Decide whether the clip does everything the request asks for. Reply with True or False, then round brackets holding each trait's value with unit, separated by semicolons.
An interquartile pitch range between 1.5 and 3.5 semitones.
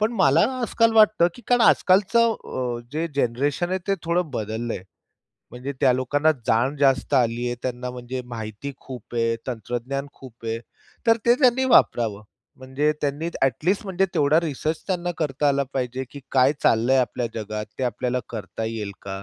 False (5.6 semitones)